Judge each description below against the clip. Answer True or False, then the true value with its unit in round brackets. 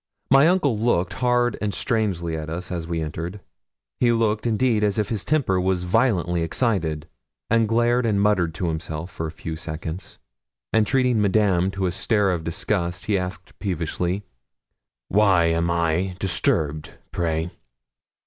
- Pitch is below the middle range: True (95 Hz)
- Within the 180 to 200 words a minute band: False (155 wpm)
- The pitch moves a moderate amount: True (4.6 semitones)